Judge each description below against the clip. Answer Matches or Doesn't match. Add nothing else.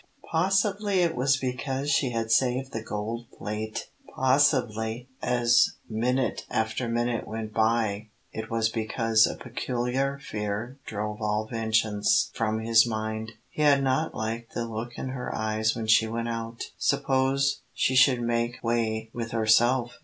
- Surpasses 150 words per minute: Doesn't match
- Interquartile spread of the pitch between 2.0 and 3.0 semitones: Matches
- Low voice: Matches